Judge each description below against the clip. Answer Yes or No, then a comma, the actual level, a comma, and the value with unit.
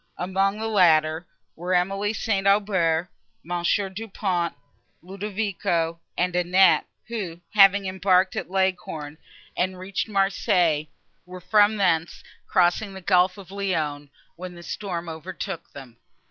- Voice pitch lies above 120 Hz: Yes, medium, 185 Hz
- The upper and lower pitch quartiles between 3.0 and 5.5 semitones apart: No, narrow, 2.5 semitones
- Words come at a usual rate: No, slow, 125 wpm